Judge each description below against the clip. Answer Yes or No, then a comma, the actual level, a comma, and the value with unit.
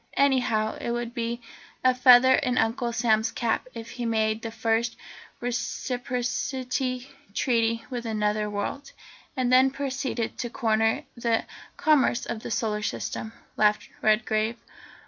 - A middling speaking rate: No, slow, 130 wpm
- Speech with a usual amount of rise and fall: No, narrow, 2.2 semitones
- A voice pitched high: Yes, high, 235 Hz